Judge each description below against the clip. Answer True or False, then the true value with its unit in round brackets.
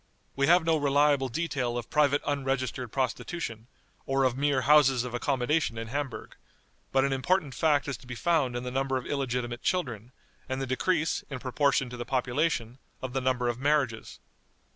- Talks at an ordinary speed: True (180 wpm)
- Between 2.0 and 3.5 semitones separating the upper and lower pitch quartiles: True (2.8 semitones)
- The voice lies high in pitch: False (135 Hz)